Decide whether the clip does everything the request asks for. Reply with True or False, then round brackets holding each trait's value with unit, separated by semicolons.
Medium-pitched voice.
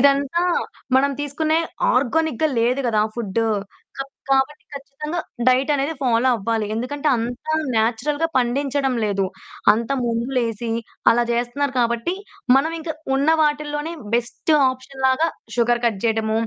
False (260 Hz)